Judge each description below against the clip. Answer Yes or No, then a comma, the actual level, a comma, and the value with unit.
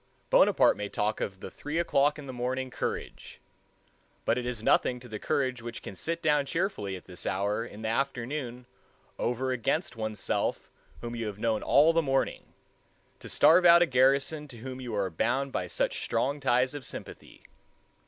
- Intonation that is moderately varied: Yes, average, 4.0 semitones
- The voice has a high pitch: No, low, 125 Hz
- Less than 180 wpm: No, average, 185 wpm